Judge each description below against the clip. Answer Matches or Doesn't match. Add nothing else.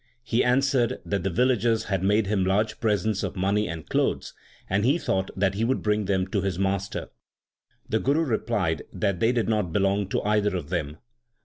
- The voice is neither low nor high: Doesn't match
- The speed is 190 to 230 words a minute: Matches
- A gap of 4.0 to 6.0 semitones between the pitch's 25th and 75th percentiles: Doesn't match